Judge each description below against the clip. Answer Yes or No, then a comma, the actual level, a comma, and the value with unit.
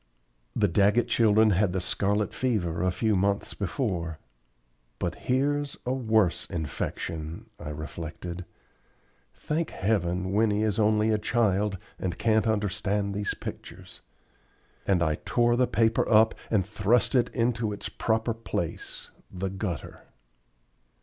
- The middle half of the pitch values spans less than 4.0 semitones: Yes, average, 3.6 semitones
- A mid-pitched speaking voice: No, low, 105 Hz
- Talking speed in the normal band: No, slow, 130 wpm